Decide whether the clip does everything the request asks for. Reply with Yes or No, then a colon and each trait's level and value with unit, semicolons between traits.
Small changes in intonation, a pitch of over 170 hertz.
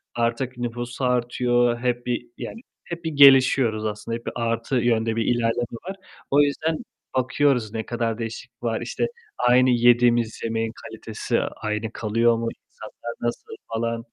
No: narrow, 1.5 semitones; low, 120 Hz